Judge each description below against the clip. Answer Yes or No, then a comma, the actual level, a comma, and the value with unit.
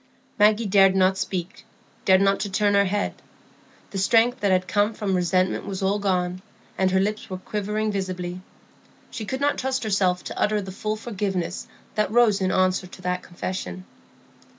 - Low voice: No, high, 195 Hz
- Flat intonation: Yes, narrow, 2.2 semitones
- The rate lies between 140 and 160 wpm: No, average, 175 wpm